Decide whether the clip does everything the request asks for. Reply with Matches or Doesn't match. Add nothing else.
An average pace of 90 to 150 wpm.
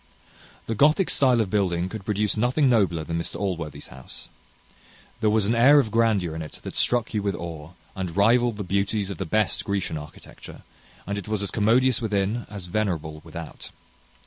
Doesn't match